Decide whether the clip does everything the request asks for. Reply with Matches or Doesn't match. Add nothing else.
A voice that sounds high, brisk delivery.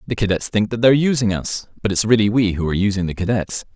Doesn't match